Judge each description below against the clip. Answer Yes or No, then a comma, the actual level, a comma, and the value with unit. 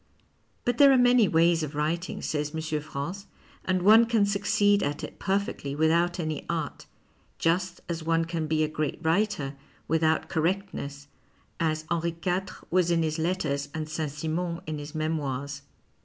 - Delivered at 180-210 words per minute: No, average, 160 wpm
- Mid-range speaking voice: Yes, medium, 165 Hz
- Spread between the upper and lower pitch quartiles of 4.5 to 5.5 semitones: No, average, 3.2 semitones